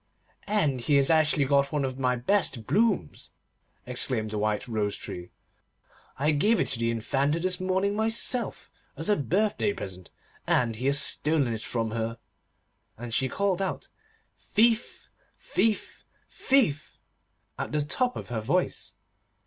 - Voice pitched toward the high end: No, medium, 140 Hz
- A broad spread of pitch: Yes, wide, 8.9 semitones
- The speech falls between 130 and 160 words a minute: Yes, average, 150 wpm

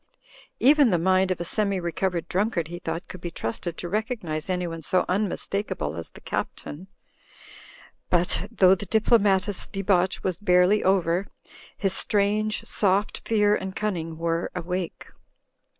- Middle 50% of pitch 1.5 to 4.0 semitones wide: Yes, average, 2.9 semitones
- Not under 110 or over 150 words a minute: Yes, average, 140 wpm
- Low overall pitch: No, medium, 185 Hz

